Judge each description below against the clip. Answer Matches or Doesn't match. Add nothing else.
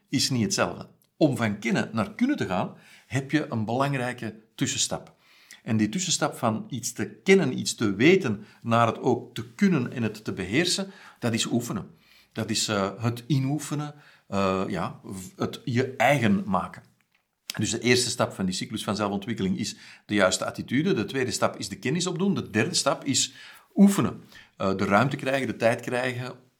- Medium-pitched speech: Doesn't match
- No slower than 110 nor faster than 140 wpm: Doesn't match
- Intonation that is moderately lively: Matches